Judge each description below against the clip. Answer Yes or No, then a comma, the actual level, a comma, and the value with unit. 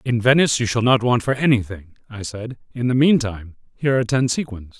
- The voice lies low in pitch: Yes, low, 120 Hz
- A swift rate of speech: Yes, fast, 225 wpm